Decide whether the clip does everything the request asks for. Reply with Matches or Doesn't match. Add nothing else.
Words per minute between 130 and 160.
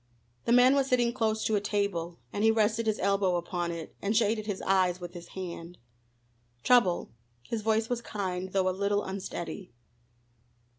Doesn't match